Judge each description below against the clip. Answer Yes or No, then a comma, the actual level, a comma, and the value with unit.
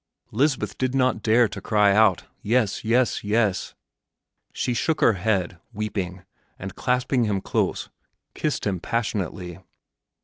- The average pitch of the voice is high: No, low, 110 Hz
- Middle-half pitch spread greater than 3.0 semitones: Yes, average, 4.0 semitones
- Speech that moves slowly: Yes, slow, 130 wpm